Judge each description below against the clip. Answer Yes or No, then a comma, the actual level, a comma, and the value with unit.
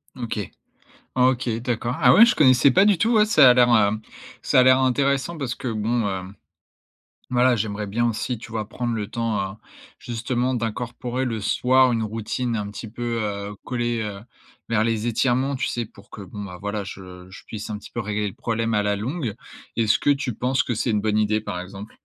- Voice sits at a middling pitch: No, low, 115 Hz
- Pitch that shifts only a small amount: No, average, 3.1 semitones